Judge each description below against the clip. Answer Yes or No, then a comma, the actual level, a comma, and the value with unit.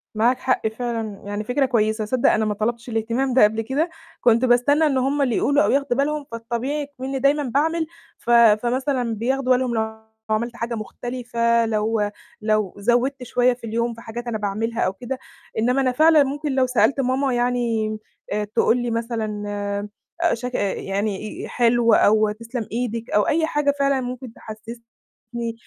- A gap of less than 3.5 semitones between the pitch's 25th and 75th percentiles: Yes, average, 2.9 semitones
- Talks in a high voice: Yes, high, 235 Hz